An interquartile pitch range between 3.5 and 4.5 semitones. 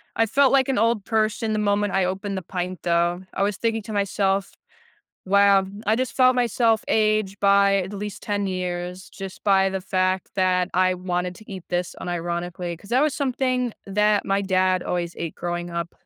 No: average, 2.8 semitones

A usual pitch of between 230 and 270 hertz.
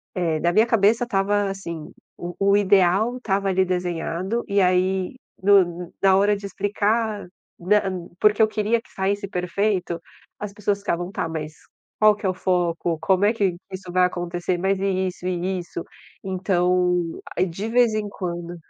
No: high, 190 Hz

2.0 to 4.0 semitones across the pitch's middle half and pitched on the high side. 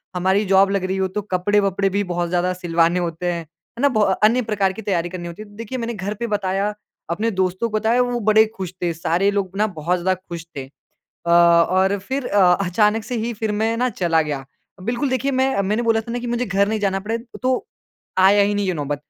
Yes: average, 3.7 semitones; high, 200 Hz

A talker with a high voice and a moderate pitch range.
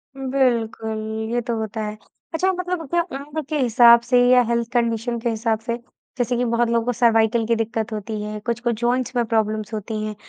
No: high, 235 Hz; narrow, 1.9 semitones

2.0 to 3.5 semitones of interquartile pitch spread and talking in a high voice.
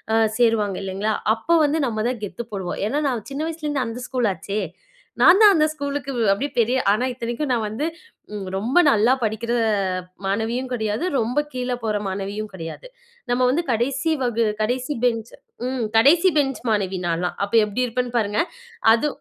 No: average, 4.0 semitones; high, 235 Hz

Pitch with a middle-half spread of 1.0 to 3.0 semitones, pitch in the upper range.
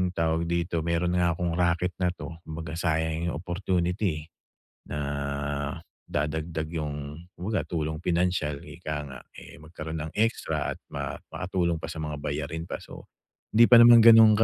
No: narrow, 2.4 semitones; very low, 85 Hz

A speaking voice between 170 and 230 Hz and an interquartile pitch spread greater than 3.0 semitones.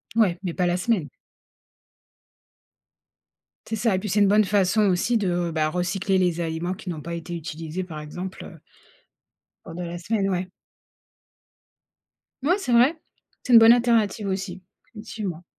Yes: medium, 185 Hz; average, 3.7 semitones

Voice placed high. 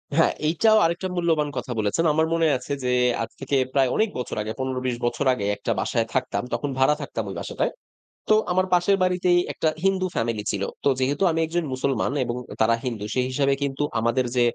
No: medium, 140 Hz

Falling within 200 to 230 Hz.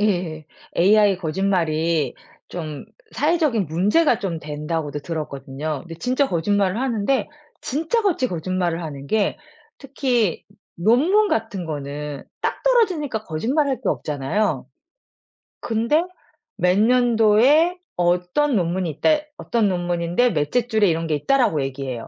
No: high, 190 Hz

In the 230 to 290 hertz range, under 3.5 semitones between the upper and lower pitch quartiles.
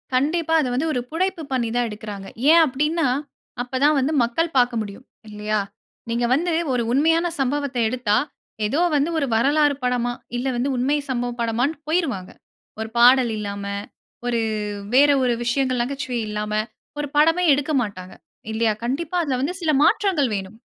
No: very high, 255 Hz; average, 4.2 semitones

